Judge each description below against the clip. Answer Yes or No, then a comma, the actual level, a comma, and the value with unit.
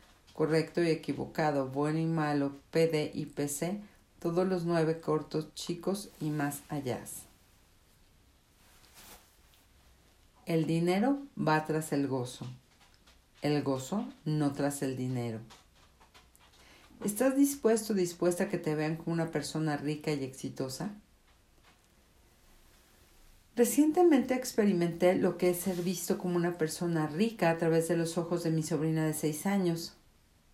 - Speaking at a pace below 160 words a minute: Yes, average, 130 wpm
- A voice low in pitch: No, medium, 155 Hz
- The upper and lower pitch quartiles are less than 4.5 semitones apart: No, average, 5.0 semitones